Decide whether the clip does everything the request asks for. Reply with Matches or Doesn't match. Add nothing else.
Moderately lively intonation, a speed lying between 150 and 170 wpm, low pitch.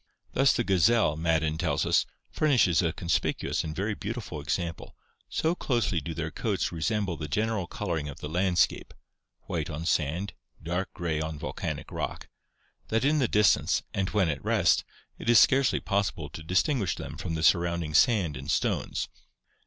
Matches